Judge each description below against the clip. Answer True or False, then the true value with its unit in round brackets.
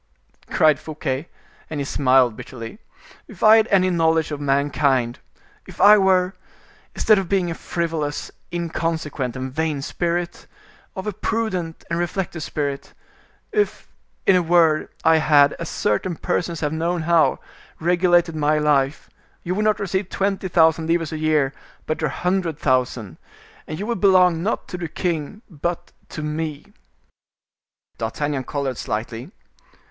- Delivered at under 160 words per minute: True (140 wpm)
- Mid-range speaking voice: True (160 Hz)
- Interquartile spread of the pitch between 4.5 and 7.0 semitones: False (3.8 semitones)